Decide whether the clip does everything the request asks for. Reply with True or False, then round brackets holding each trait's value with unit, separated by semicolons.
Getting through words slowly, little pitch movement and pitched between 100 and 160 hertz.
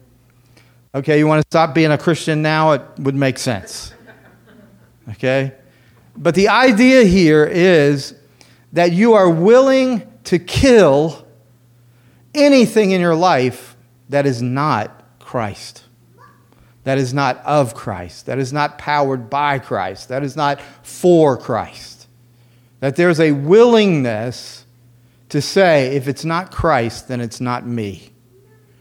False (130 wpm; 4.7 semitones; 135 Hz)